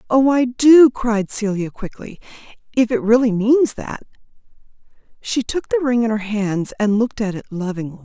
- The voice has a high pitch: Yes, high, 225 Hz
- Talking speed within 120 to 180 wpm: Yes, average, 170 wpm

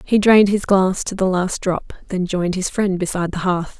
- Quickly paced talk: Yes, fast, 235 wpm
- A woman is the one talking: Yes, female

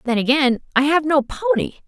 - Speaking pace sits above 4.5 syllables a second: Yes, 5.0 syllables/s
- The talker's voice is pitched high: Yes, very high, 285 Hz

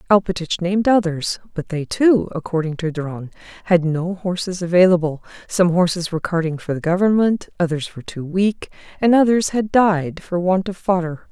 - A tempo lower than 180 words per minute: Yes, average, 170 wpm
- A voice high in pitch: No, medium, 180 Hz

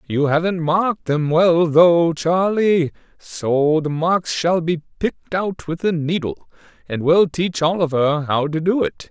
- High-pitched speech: No, medium, 165 Hz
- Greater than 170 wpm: No, average, 165 wpm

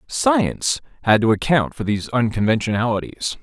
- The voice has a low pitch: Yes, low, 120 Hz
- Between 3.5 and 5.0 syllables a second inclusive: No, 5.3 syllables/s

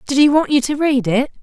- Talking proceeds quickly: Yes, fast, 295 wpm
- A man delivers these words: No, female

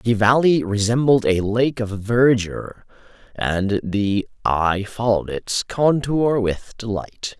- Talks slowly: Yes, slow, 120 wpm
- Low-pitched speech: Yes, low, 110 Hz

